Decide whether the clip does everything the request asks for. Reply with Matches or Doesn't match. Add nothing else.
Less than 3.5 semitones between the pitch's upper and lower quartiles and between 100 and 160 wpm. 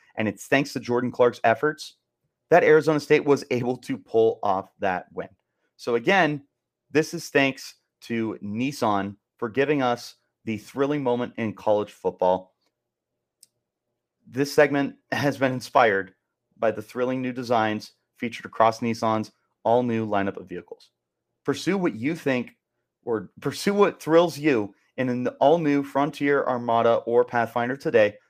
Doesn't match